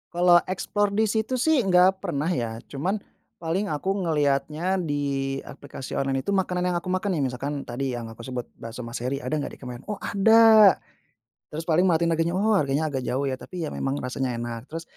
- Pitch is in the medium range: Yes, medium, 160 Hz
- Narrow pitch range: No, wide, 5.6 semitones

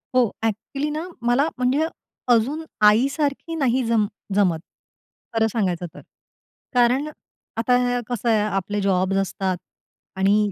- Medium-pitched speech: No, high, 235 Hz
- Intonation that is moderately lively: Yes, average, 4.6 semitones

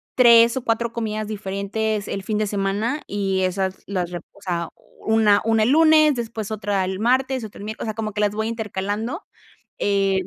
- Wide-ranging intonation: No, narrow, 2.6 semitones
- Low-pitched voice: No, high, 215 Hz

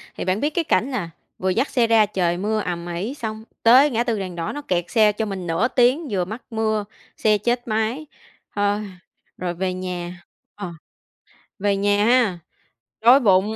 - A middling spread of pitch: Yes, average, 4.1 semitones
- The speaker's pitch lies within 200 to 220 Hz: Yes, high, 210 Hz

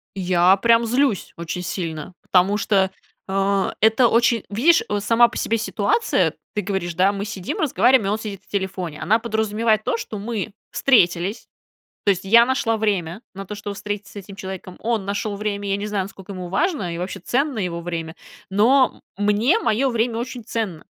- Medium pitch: No, high, 205 Hz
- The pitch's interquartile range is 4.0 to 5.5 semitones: No, average, 3.2 semitones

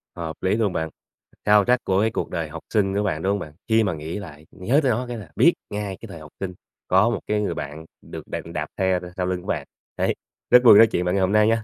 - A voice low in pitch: Yes, very low, 95 Hz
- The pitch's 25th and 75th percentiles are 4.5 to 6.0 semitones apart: No, average, 3.9 semitones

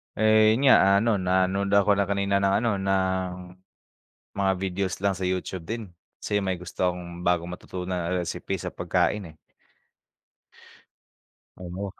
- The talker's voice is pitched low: Yes, very low, 95 Hz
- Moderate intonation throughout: No, narrow, 1.7 semitones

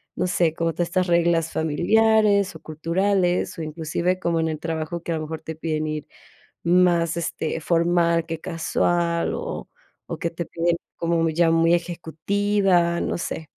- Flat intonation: Yes, narrow, 1.4 semitones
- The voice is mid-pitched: Yes, medium, 170 Hz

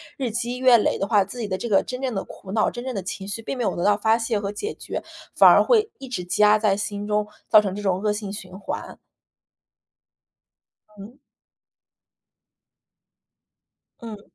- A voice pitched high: Yes, high, 210 Hz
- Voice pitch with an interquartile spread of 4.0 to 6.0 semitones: No, average, 2.9 semitones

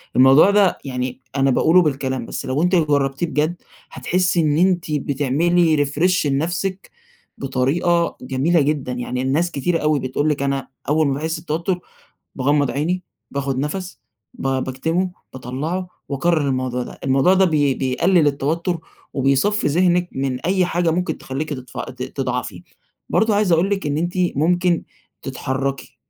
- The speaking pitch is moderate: Yes, medium, 150 Hz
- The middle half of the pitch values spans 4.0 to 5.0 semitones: Yes, average, 4.4 semitones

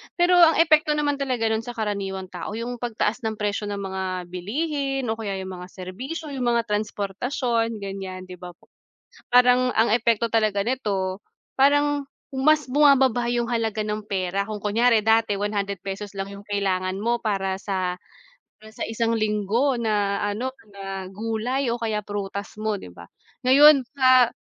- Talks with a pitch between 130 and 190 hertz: No, high, 220 Hz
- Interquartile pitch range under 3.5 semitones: No, average, 4.0 semitones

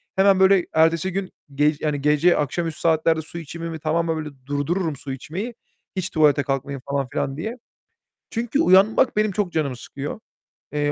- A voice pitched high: No, medium, 160 Hz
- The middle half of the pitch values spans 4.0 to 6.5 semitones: Yes, average, 4.4 semitones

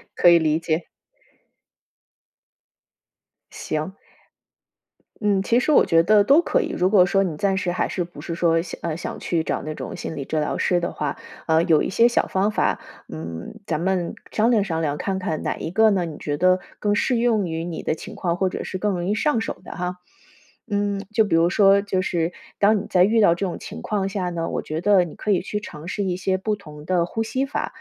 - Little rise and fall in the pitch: No, average, 3.7 semitones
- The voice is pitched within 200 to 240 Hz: No, medium, 185 Hz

